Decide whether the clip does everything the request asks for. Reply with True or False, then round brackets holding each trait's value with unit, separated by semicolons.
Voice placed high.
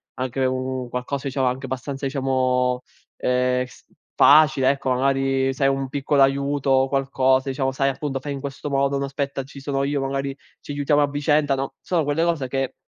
False (135 Hz)